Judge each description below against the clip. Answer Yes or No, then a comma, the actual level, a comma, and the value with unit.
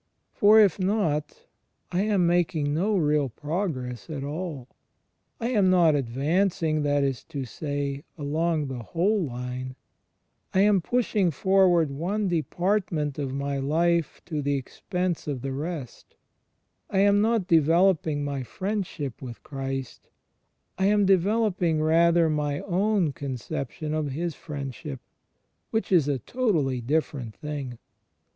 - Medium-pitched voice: Yes, medium, 155 Hz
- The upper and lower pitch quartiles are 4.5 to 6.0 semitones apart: Yes, average, 4.9 semitones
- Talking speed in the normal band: No, slow, 130 wpm